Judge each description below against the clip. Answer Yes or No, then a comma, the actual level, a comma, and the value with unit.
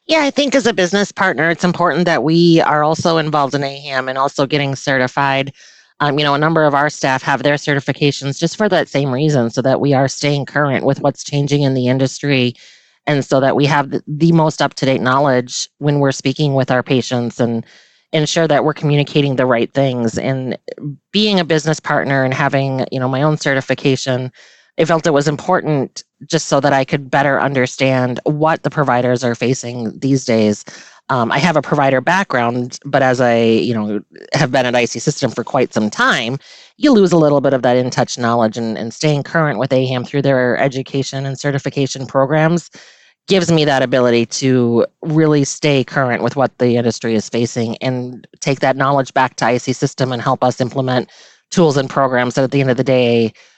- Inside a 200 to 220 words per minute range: Yes, fast, 205 wpm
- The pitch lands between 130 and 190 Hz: Yes, low, 135 Hz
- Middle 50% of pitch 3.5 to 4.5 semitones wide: No, average, 2.9 semitones